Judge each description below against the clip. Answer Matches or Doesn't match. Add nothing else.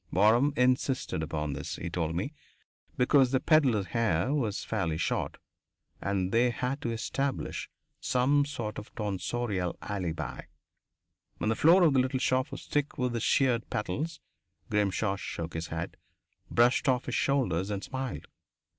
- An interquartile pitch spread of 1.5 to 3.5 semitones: Doesn't match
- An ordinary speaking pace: Matches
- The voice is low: Matches